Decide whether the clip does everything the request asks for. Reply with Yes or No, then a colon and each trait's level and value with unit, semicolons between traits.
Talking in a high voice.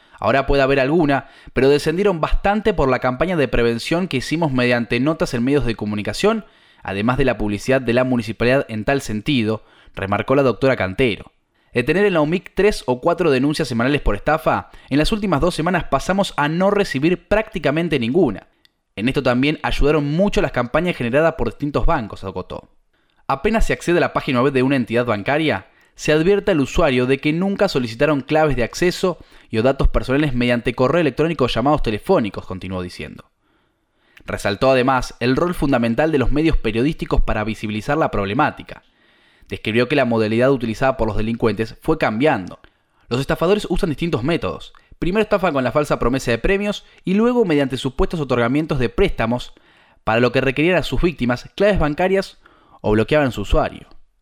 No: medium, 140 Hz